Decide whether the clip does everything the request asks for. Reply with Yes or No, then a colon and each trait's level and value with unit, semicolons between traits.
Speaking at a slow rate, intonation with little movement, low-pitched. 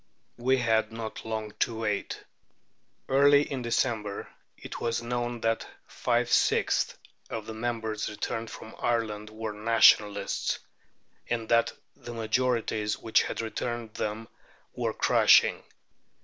Yes: slow, 120 wpm; narrow, 1.6 semitones; low, 115 Hz